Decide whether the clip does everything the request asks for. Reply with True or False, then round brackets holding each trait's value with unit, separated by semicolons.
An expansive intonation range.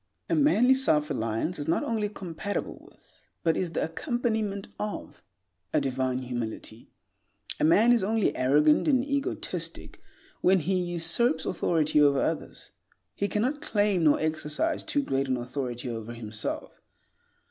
True (8.0 semitones)